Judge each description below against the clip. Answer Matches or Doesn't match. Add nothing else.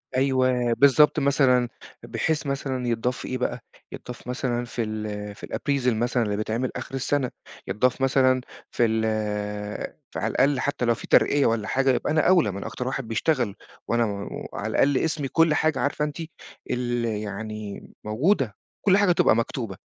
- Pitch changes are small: Doesn't match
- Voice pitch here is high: Doesn't match